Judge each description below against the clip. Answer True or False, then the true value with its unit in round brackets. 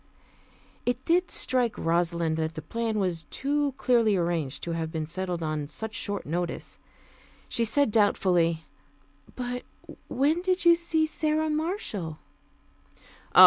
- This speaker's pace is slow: True (130 wpm)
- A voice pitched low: False (210 Hz)